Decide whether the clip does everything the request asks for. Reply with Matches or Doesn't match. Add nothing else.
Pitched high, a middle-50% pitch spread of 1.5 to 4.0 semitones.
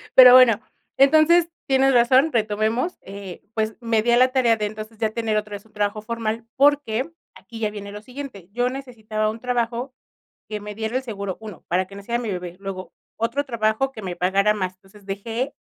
Matches